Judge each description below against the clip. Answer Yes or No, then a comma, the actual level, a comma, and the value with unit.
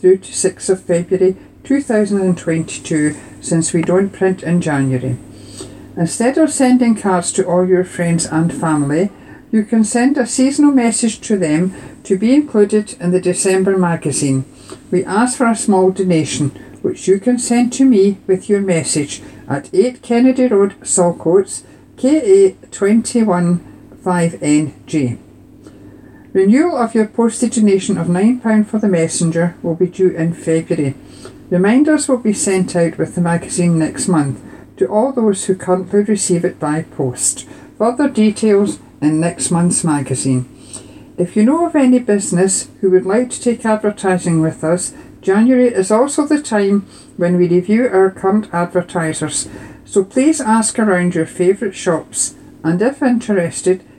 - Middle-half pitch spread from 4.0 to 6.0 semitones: Yes, average, 5.1 semitones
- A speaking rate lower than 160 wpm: Yes, average, 150 wpm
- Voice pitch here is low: No, high, 190 Hz